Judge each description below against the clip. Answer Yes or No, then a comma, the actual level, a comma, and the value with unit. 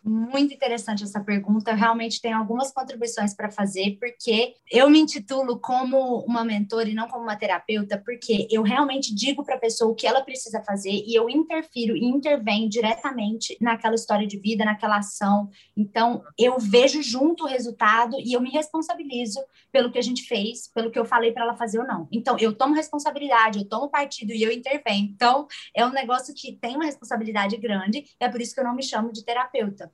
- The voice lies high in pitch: Yes, high, 235 Hz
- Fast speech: Yes, fast, 200 wpm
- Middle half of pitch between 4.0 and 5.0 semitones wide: No, average, 3.2 semitones